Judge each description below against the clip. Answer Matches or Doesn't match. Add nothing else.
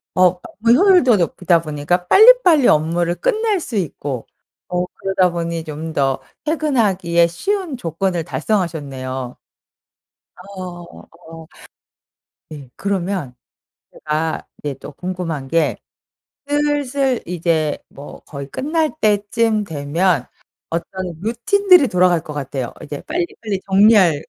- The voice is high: Doesn't match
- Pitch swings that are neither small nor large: Doesn't match